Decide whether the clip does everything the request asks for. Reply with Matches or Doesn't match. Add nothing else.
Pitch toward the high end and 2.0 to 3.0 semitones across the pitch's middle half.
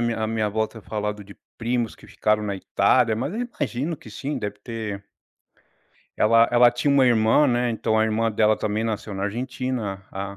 Doesn't match